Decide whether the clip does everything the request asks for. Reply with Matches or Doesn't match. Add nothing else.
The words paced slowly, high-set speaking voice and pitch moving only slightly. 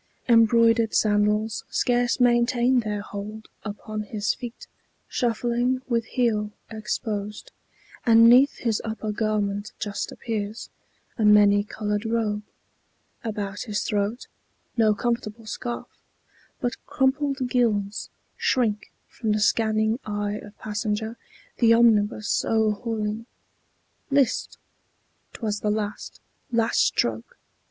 Matches